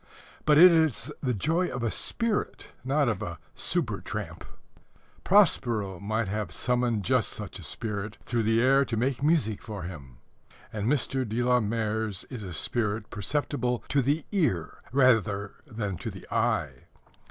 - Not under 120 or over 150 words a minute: No, average, 160 wpm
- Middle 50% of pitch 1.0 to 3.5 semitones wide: No, average, 4.6 semitones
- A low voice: Yes, low, 115 Hz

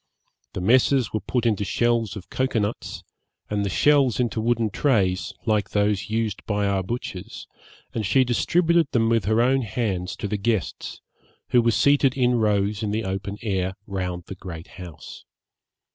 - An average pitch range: Yes, average, 3.6 semitones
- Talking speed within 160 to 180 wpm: Yes, average, 170 wpm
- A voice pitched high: No, low, 110 Hz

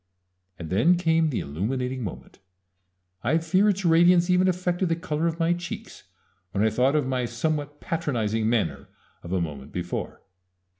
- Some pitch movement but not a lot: No, wide, 7.4 semitones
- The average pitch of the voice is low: No, medium, 150 Hz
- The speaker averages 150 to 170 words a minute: Yes, average, 160 wpm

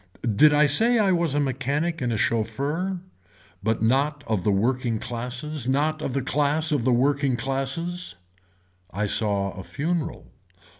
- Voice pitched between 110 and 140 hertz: Yes, low, 135 Hz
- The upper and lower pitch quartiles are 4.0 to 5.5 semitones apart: Yes, average, 4.4 semitones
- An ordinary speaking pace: Yes, average, 155 wpm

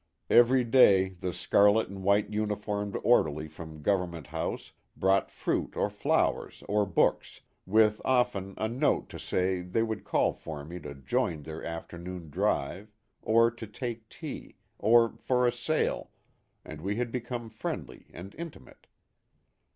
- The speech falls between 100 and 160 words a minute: Yes, average, 145 wpm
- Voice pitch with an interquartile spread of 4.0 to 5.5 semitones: Yes, average, 4.6 semitones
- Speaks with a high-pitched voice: No, low, 100 Hz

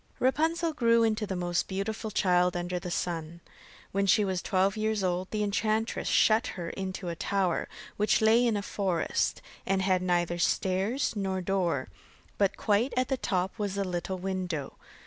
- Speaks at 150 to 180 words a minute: Yes, average, 170 wpm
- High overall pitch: Yes, high, 195 Hz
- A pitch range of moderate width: Yes, average, 3.2 semitones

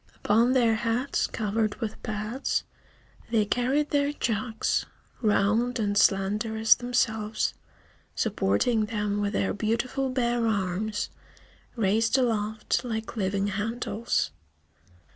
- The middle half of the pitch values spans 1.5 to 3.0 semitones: Yes, narrow, 2.5 semitones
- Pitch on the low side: No, high, 220 Hz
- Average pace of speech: No, slow, 105 wpm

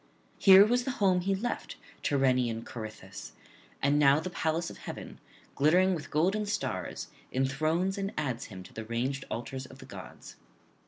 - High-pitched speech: No, medium, 150 Hz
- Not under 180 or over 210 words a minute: No, average, 155 wpm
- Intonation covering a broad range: Yes, wide, 6.8 semitones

